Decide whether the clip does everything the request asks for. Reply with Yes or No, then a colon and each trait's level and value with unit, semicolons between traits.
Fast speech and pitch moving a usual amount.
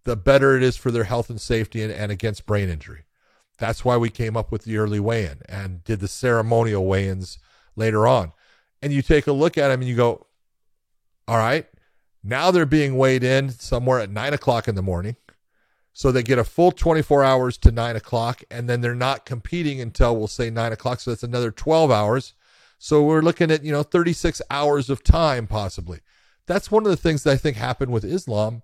Yes: fast, 215 wpm; average, 4.4 semitones